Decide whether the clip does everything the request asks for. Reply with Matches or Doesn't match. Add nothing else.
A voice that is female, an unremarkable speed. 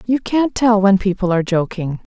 Matches